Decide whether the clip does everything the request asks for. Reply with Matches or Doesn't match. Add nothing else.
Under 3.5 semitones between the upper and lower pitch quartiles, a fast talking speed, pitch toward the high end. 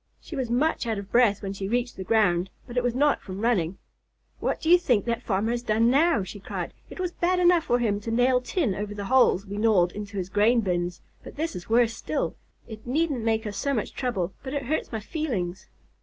Doesn't match